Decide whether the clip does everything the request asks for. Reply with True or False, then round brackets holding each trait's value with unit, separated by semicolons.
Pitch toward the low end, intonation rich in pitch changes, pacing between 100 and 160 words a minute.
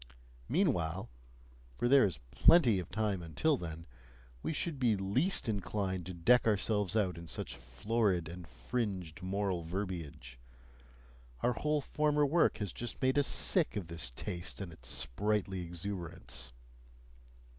True (95 Hz; 6.0 semitones; 140 wpm)